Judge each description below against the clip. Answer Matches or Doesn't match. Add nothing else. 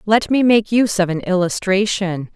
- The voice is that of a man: Doesn't match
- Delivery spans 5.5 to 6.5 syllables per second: Doesn't match